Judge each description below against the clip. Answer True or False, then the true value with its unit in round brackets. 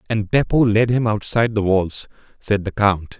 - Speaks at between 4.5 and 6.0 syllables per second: True (4.8 syllables/s)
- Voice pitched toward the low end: True (105 Hz)